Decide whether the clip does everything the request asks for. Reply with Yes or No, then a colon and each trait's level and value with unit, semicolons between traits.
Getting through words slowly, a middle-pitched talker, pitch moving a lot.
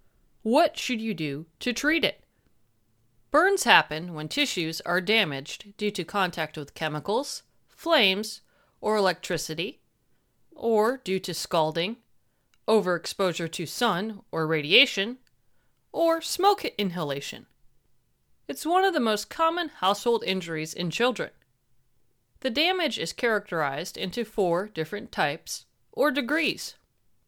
No: slow, 115 wpm; high, 205 Hz; wide, 7.4 semitones